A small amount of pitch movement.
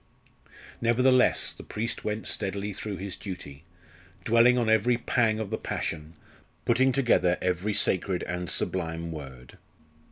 No: average, 4.8 semitones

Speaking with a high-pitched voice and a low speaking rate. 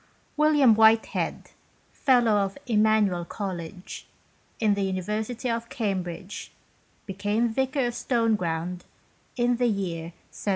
Yes: high, 215 Hz; slow, 110 wpm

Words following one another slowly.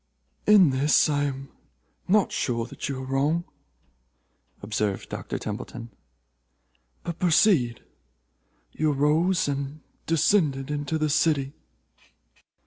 Yes: slow, 105 wpm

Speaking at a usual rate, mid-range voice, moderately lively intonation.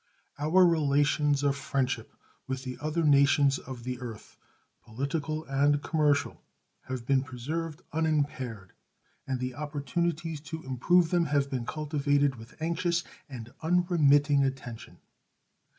No: slow, 120 wpm; medium, 145 Hz; average, 3.0 semitones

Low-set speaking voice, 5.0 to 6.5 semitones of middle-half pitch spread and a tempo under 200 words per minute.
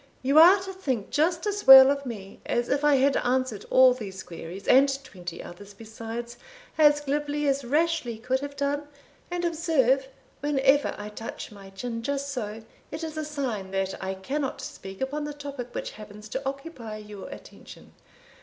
No: very high, 265 Hz; average, 5.3 semitones; average, 175 wpm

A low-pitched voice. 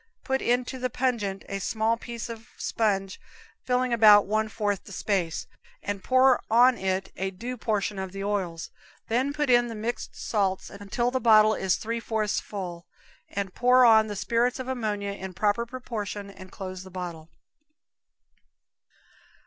No: high, 215 Hz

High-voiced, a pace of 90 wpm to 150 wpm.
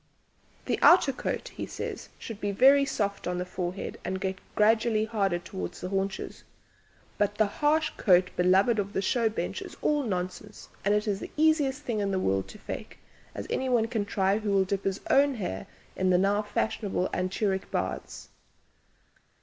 No: high, 205 Hz; average, 175 wpm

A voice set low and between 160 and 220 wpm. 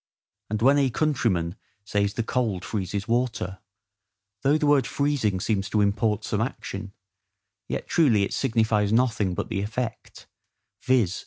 No: low, 110 Hz; average, 145 wpm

